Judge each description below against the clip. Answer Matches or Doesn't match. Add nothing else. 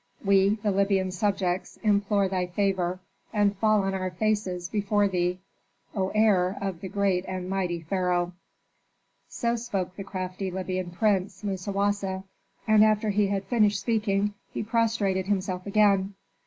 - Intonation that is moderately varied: Doesn't match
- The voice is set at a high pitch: Matches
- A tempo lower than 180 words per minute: Matches